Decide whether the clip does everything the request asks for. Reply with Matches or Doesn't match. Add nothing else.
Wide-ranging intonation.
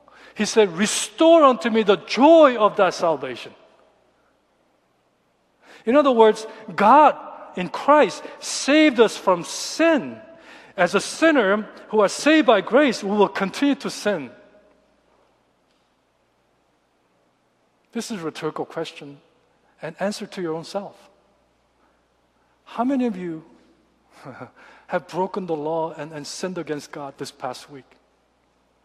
Matches